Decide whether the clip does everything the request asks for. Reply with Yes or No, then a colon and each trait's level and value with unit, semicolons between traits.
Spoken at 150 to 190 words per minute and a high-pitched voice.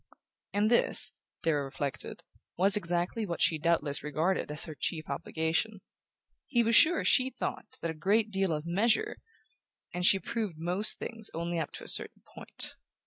No: average, 160 wpm; medium, 175 Hz